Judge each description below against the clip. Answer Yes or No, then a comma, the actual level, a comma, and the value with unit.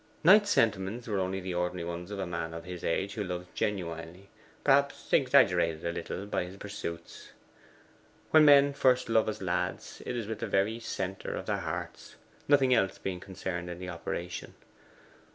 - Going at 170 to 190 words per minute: Yes, average, 175 wpm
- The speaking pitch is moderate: No, very low, 95 Hz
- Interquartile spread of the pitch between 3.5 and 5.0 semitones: Yes, average, 4.4 semitones